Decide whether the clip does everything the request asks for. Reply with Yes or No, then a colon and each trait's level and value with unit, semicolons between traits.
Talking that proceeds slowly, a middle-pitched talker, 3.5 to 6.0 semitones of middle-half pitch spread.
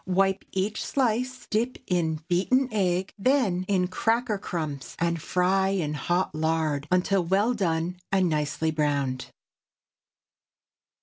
Yes: slow, 120 wpm; medium, 180 Hz; average, 3.8 semitones